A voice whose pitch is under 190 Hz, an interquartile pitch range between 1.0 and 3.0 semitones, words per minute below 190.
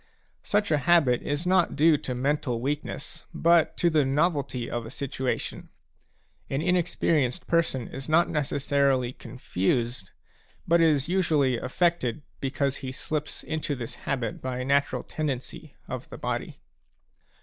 No: medium, 140 Hz; average, 3.8 semitones; slow, 135 wpm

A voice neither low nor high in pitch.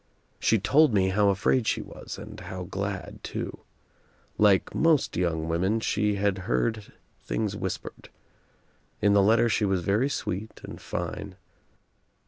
No: low, 100 Hz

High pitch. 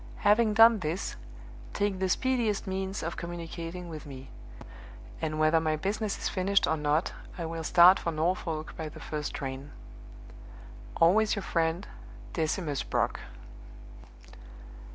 No: medium, 170 Hz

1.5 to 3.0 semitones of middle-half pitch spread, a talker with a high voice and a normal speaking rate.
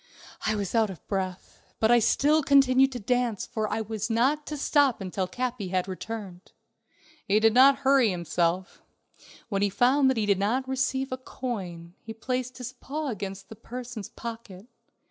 No: average, 4.6 semitones; high, 225 Hz; average, 175 wpm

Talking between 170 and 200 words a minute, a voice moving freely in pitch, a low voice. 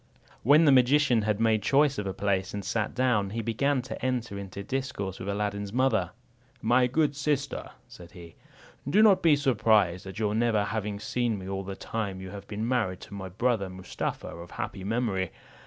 No: average, 190 wpm; average, 4.5 semitones; low, 110 Hz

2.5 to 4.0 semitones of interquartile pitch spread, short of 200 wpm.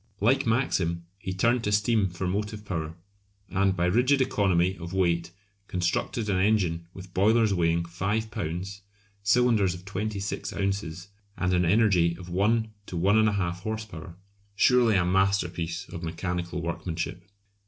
Yes: average, 3.4 semitones; average, 145 wpm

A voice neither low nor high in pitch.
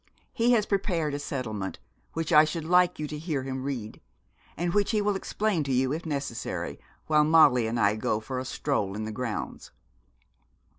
Yes: medium, 150 Hz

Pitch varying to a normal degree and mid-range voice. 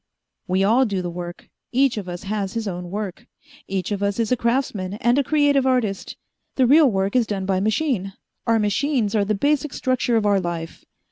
No: average, 4.7 semitones; high, 210 Hz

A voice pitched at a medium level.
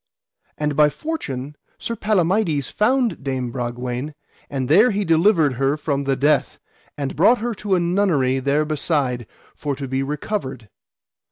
Yes: medium, 150 Hz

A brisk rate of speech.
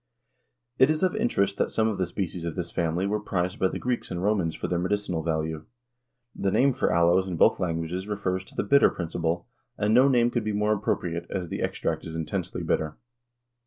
Yes: fast, 210 wpm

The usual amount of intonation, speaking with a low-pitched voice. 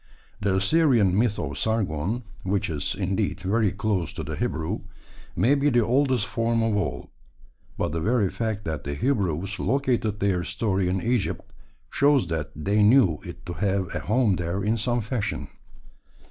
Yes: average, 4.1 semitones; low, 105 Hz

